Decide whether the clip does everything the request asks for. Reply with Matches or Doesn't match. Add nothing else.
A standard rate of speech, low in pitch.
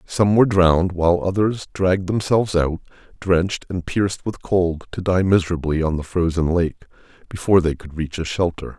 Matches